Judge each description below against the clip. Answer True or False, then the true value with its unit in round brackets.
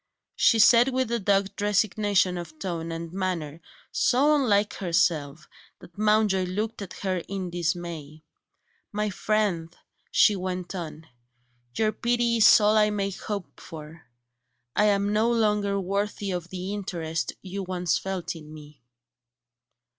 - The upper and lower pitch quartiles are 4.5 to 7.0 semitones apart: False (3.5 semitones)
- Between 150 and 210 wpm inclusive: False (140 wpm)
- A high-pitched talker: True (195 Hz)